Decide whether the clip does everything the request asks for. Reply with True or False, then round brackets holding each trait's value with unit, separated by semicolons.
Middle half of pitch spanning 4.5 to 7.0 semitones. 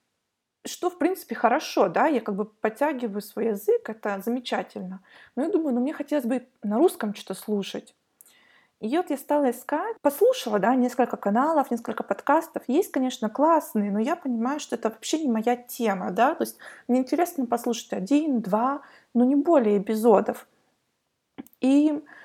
True (4.8 semitones)